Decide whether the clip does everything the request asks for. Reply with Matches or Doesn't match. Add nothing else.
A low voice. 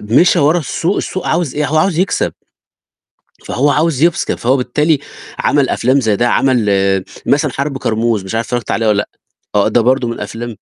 Matches